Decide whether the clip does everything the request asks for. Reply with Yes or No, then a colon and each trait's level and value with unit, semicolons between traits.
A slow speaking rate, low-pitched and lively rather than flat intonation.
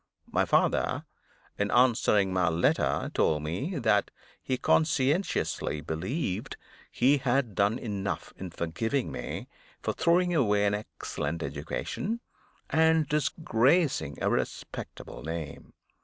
Yes: slow, 110 wpm; low, 115 Hz; wide, 7.6 semitones